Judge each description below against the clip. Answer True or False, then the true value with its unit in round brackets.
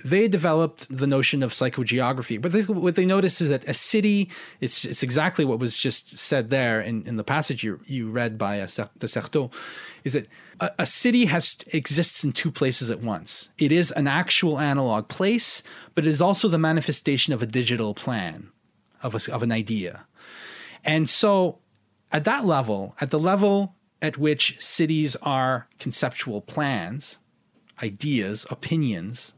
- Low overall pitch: False (145 Hz)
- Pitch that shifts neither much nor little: False (5.7 semitones)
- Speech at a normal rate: True (170 wpm)